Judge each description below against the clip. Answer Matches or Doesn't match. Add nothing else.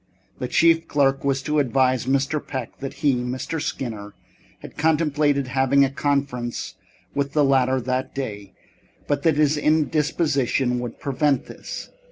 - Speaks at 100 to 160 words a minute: Matches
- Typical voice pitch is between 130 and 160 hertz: Matches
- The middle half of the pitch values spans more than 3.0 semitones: Doesn't match